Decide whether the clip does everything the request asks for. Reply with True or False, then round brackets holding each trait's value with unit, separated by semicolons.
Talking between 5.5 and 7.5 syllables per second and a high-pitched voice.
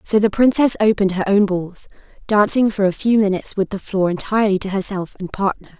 True (6.0 syllables/s; 200 Hz)